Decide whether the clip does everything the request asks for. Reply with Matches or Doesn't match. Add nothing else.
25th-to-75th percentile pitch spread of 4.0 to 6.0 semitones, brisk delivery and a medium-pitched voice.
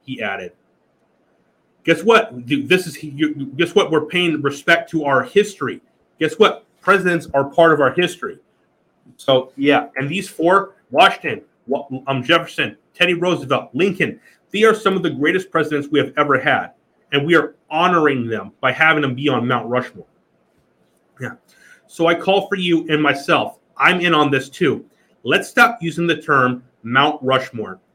Doesn't match